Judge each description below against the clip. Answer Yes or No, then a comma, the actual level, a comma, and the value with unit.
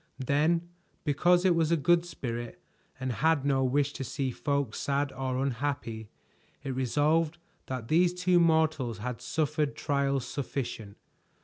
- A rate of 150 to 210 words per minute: No, average, 140 wpm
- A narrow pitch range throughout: No, average, 3.7 semitones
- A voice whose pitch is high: No, medium, 140 Hz